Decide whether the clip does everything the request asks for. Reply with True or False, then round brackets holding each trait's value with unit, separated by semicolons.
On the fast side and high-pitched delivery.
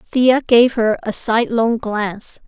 False (145 wpm; 230 Hz)